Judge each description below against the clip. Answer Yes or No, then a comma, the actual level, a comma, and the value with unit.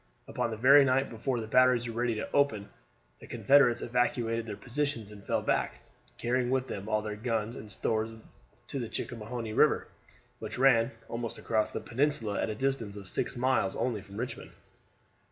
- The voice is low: Yes, low, 115 Hz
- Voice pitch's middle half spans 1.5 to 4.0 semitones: Yes, average, 2.8 semitones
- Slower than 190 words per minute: Yes, average, 180 wpm